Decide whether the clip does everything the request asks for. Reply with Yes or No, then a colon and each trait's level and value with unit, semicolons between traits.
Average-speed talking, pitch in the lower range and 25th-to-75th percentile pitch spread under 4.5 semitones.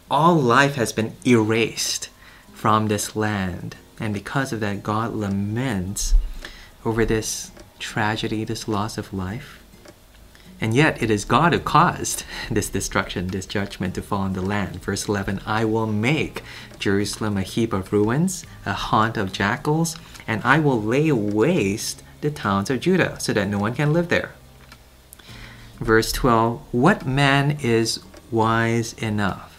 Yes: average, 150 wpm; low, 110 Hz; average, 3.0 semitones